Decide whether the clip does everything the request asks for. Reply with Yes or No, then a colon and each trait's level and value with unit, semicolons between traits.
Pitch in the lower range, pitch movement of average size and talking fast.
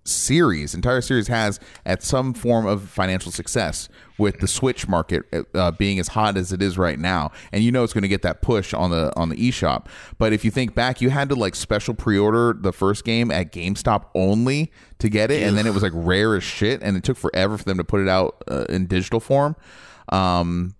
Yes: low, 100 Hz; average, 4.0 semitones; fast, 230 wpm